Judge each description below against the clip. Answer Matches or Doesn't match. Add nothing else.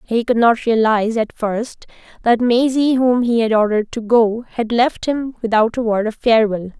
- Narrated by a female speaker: Matches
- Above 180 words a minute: Matches